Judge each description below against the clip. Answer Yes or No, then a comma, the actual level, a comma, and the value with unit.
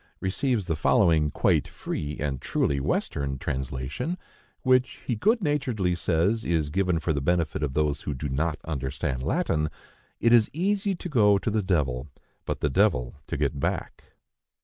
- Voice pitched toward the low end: Yes, very low, 80 Hz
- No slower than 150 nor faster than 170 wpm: Yes, average, 160 wpm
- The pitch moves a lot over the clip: Yes, wide, 7.4 semitones